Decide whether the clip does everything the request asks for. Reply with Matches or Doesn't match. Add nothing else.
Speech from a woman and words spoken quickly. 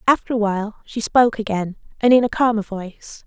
Doesn't match